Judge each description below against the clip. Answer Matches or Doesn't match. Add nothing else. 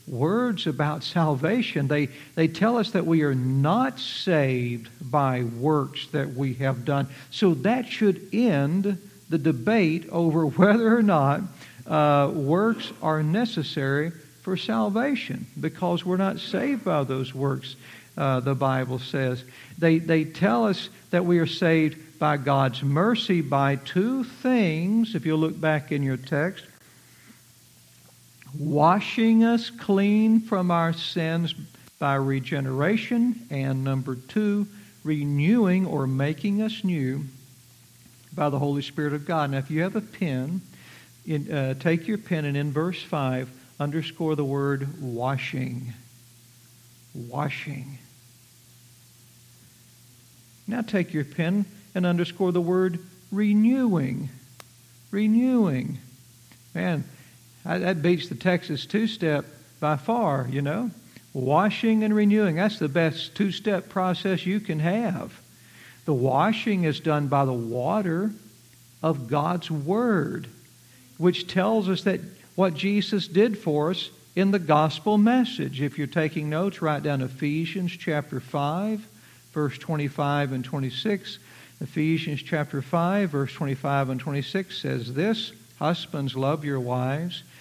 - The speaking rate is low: Matches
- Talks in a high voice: Doesn't match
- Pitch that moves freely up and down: Matches